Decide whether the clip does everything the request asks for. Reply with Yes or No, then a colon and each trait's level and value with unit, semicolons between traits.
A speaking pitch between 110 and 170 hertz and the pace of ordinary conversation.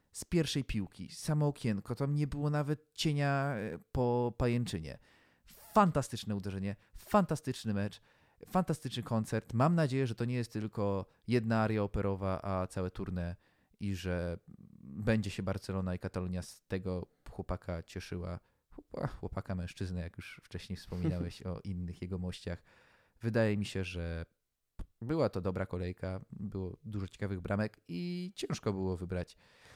No: low, 100 Hz; average, 135 wpm